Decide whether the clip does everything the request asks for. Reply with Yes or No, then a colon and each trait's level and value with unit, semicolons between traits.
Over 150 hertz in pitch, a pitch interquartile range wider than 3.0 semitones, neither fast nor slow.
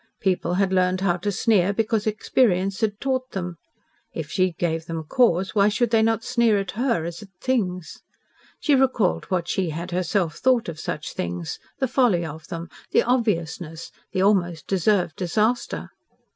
Yes: high, 190 Hz; average, 4.5 semitones; average, 170 wpm